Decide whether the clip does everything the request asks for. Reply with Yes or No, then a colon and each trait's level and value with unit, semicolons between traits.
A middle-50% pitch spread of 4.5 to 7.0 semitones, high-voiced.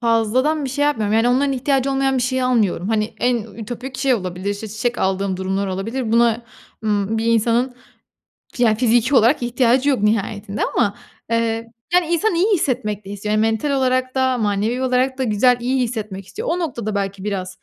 No: average, 3.6 semitones; high, 230 Hz